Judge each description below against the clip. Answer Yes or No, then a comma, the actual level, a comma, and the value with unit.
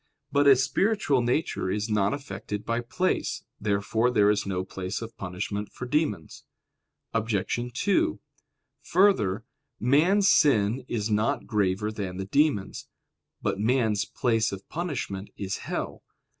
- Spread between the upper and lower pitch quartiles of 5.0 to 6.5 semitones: Yes, average, 5.3 semitones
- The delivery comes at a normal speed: No, slow, 130 wpm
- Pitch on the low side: Yes, low, 110 Hz